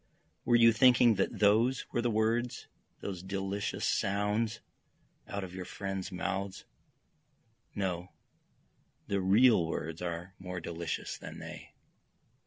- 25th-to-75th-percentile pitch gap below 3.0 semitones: No, average, 3.4 semitones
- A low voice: Yes, low, 100 Hz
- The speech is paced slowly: Yes, slow, 120 wpm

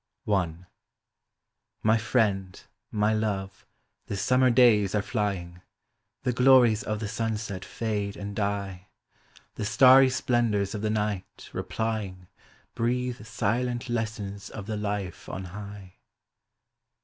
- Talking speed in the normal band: No, slow, 115 wpm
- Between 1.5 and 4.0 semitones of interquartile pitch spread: Yes, average, 2.7 semitones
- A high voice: No, low, 105 Hz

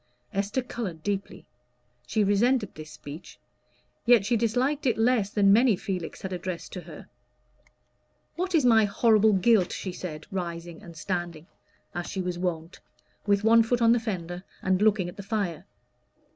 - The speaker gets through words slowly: No, average, 160 wpm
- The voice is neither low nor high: No, high, 200 Hz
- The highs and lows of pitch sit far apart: No, average, 4.3 semitones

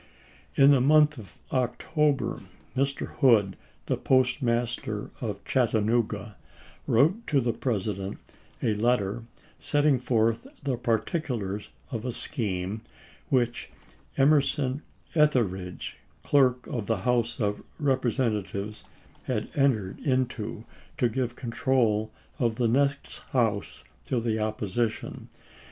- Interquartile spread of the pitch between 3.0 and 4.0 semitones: Yes, average, 3.7 semitones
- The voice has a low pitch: Yes, low, 120 Hz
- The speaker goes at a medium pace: No, slow, 110 wpm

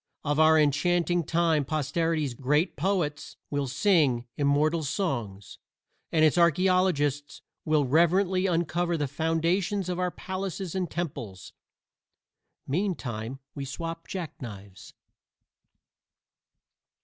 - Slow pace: Yes, slow, 100 wpm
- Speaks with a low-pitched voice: No, medium, 160 Hz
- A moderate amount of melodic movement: Yes, average, 3.7 semitones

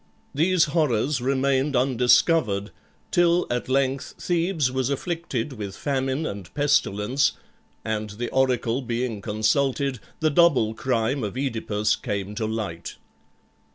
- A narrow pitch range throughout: No, average, 4.4 semitones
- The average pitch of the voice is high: No, low, 130 Hz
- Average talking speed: No, slow, 120 wpm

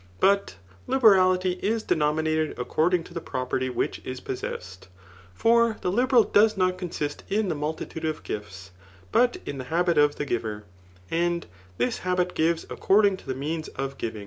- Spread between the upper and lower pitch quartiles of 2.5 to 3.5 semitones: No, wide, 5.5 semitones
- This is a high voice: No, medium, 165 Hz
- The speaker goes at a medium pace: Yes, average, 170 wpm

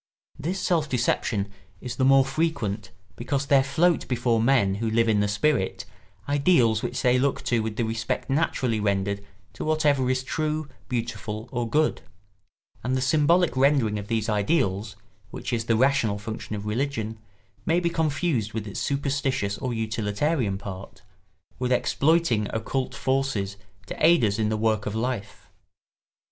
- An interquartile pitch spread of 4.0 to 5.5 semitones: Yes, average, 4.7 semitones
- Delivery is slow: No, average, 155 wpm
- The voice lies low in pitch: Yes, low, 120 Hz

